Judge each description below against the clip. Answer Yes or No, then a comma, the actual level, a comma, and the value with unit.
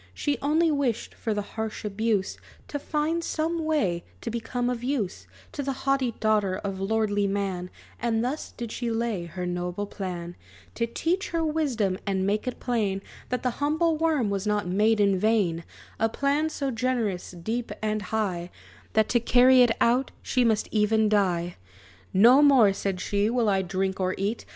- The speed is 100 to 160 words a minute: No, average, 175 wpm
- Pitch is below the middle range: No, high, 220 Hz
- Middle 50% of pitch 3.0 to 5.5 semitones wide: Yes, average, 4.6 semitones